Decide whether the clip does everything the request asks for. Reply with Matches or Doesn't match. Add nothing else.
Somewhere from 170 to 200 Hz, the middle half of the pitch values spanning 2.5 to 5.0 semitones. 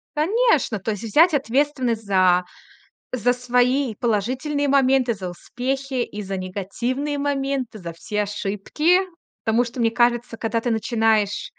Doesn't match